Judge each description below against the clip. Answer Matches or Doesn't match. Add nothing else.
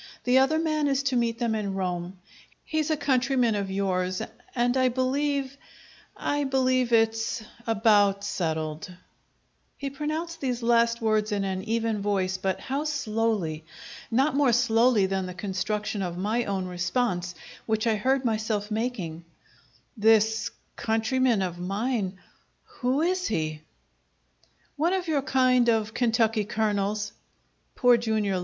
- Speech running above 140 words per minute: Doesn't match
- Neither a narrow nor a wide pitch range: Matches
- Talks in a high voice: Matches